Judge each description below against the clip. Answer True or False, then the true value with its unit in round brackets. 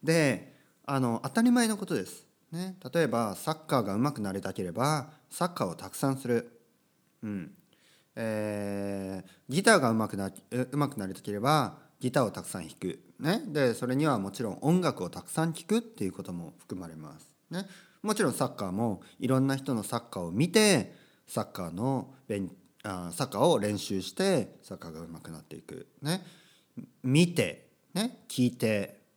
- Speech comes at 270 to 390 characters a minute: True (335 characters per minute)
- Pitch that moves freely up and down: True (8.6 semitones)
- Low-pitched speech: True (130 Hz)